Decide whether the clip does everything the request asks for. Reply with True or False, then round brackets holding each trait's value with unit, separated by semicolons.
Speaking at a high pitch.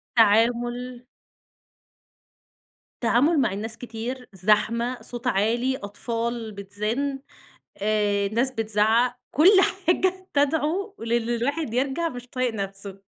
True (240 Hz)